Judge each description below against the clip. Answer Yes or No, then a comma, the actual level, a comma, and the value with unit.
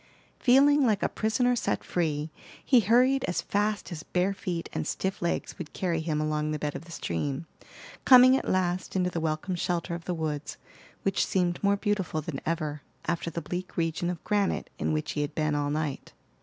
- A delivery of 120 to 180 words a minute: No, average, 195 wpm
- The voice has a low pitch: No, medium, 175 Hz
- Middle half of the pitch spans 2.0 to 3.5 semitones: No, average, 4.5 semitones